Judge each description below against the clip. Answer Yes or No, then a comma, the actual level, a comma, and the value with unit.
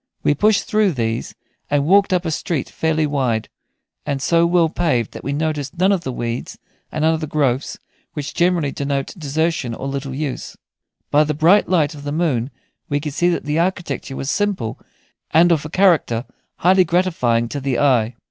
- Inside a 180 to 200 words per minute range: Yes, average, 185 wpm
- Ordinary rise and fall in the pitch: Yes, average, 4.0 semitones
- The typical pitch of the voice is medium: Yes, medium, 150 Hz